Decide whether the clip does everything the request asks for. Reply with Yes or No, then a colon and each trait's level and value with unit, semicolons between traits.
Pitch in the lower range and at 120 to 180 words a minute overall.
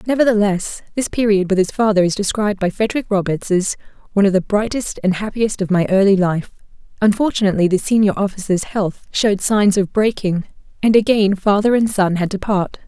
No: high, 200 Hz; average, 175 wpm